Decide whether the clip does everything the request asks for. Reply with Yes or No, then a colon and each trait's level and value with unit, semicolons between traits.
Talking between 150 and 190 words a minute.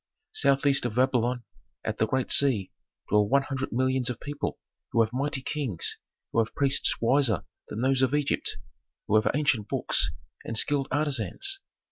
Yes: average, 160 wpm